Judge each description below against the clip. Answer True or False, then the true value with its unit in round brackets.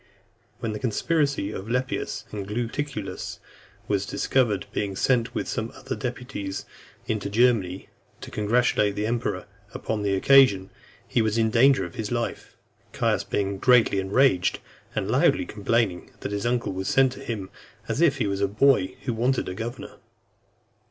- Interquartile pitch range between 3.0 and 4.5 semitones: True (3.9 semitones)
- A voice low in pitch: True (110 Hz)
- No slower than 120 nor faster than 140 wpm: False (160 wpm)